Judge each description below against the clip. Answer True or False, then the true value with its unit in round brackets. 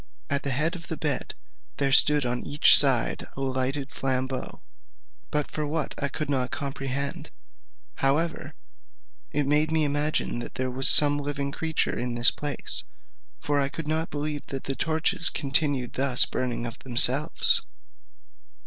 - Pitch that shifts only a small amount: True (2.2 semitones)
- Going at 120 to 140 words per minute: False (160 wpm)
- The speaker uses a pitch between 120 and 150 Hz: True (140 Hz)